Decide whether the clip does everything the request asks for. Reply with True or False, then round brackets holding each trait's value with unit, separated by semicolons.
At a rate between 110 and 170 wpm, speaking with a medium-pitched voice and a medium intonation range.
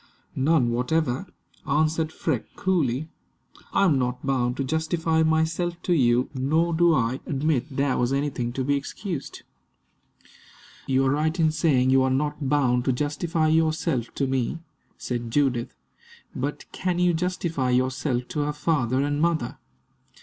True (150 wpm; 145 Hz; 3.7 semitones)